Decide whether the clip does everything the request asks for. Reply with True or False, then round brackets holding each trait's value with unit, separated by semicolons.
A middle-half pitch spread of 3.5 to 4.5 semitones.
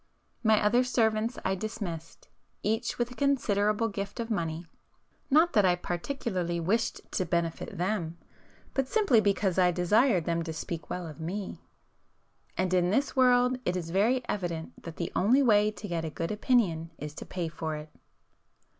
False (5.2 semitones)